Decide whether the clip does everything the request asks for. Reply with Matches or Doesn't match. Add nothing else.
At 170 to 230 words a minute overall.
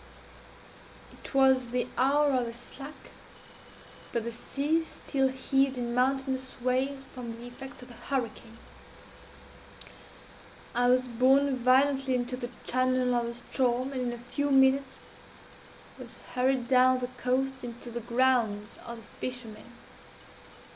Doesn't match